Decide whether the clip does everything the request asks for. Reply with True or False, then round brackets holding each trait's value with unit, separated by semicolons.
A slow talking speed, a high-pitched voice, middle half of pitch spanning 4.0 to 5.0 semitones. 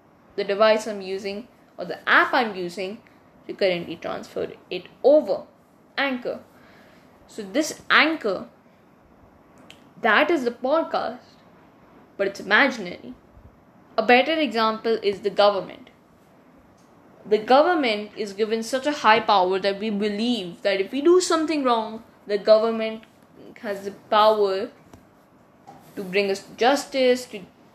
True (125 wpm; 220 Hz; 4.6 semitones)